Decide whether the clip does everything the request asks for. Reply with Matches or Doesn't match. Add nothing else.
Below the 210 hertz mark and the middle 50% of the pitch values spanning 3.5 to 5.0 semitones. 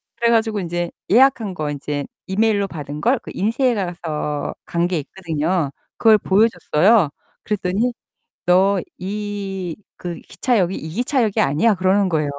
Matches